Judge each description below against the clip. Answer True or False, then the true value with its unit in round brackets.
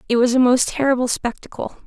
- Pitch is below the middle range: False (250 Hz)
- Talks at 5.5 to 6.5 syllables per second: True (6.2 syllables/s)